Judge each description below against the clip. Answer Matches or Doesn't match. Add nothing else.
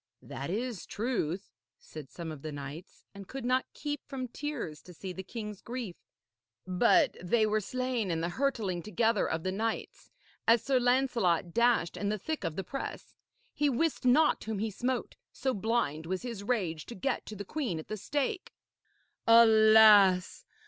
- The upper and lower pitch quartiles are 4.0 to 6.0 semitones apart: Matches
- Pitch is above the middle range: Matches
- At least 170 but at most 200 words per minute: Matches